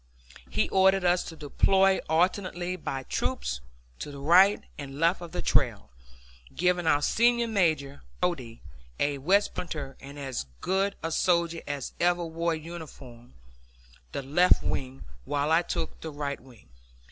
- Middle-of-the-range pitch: Yes, medium, 165 Hz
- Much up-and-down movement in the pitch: No, average, 4.3 semitones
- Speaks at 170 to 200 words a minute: No, average, 150 wpm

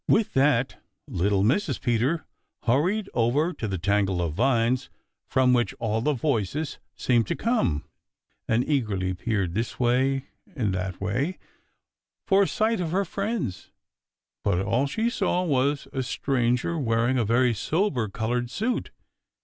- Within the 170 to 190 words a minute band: No, average, 145 wpm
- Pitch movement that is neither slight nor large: No, wide, 5.8 semitones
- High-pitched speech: No, low, 125 Hz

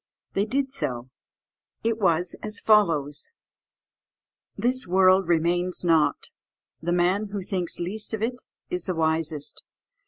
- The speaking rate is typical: No, slow, 125 wpm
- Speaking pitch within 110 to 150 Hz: No, medium, 180 Hz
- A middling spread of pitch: Yes, average, 4.3 semitones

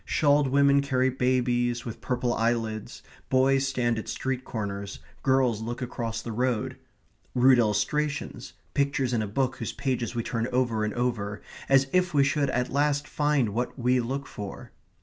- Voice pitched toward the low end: Yes, low, 125 Hz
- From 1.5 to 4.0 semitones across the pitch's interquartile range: Yes, average, 2.8 semitones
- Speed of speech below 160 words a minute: No, average, 165 wpm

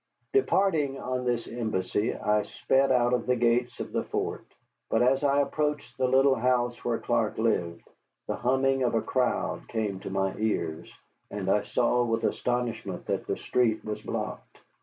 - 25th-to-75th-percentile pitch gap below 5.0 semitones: Yes, average, 3.2 semitones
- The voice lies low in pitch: Yes, low, 120 Hz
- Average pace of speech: Yes, average, 170 wpm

